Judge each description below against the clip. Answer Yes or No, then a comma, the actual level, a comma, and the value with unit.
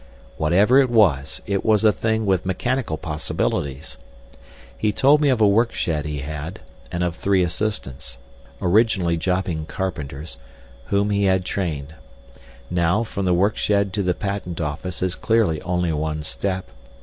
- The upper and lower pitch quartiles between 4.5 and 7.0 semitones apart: Yes, average, 4.9 semitones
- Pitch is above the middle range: No, very low, 90 Hz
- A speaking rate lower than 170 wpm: Yes, average, 150 wpm